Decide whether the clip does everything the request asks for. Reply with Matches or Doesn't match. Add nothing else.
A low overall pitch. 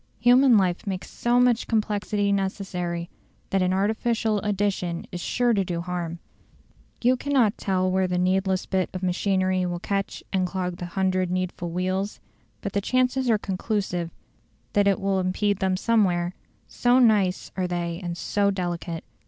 Doesn't match